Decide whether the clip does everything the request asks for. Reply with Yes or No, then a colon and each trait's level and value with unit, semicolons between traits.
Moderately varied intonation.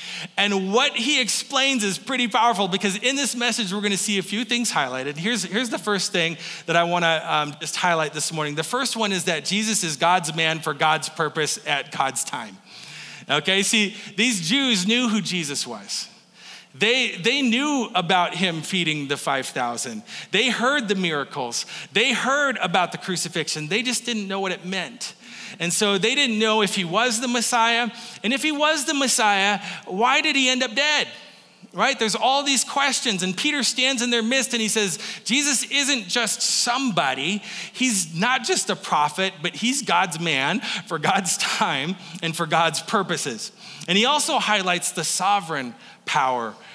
No: wide, 5.8 semitones